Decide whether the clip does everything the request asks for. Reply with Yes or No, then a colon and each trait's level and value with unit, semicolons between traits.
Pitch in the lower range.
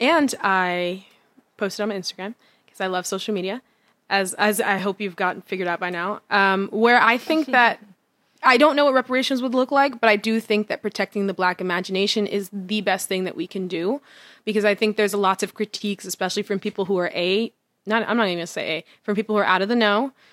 No: high, 205 Hz